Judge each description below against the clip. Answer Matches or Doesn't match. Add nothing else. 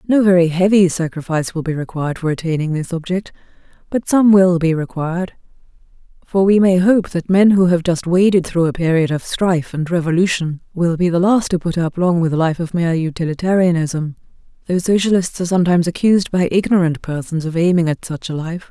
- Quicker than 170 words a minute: Matches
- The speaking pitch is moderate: Matches